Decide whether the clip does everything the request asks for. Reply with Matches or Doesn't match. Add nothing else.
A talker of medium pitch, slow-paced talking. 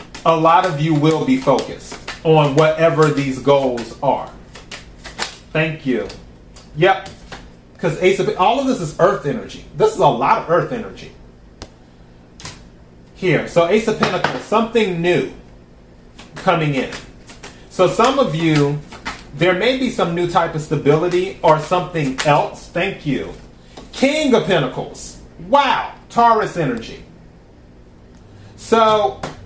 Matches